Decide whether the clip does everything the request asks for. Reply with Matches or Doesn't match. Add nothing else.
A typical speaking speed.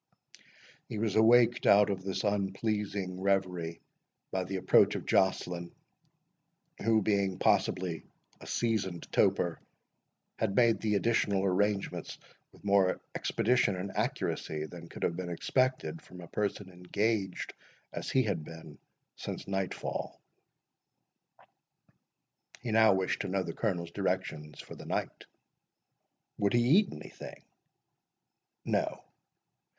Doesn't match